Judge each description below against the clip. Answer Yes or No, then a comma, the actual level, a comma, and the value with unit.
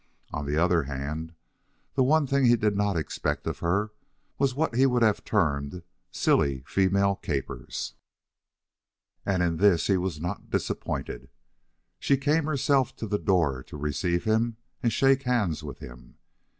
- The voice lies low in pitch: Yes, low, 100 Hz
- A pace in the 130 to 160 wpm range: Yes, average, 155 wpm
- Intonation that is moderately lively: No, wide, 7.4 semitones